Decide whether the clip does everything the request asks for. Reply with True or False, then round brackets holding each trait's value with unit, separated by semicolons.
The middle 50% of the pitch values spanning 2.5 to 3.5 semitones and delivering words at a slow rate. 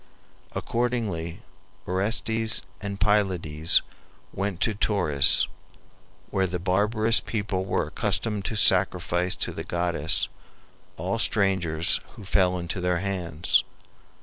True (3.0 semitones; 105 wpm)